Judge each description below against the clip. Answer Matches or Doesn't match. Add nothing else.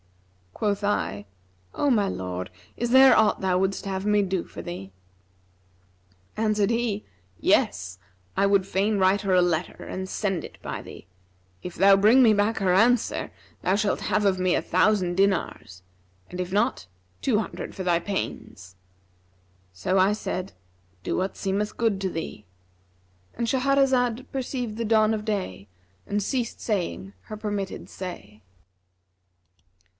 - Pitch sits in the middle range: Doesn't match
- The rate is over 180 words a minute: Doesn't match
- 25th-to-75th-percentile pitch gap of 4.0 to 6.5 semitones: Doesn't match